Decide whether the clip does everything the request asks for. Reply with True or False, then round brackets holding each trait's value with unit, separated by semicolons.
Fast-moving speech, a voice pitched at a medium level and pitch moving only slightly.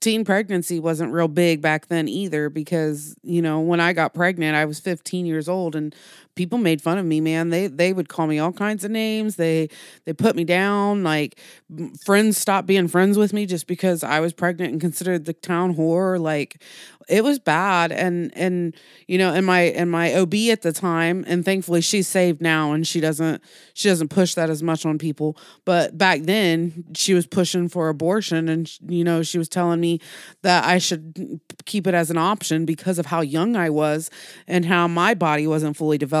True (210 wpm; 170 Hz; 2.3 semitones)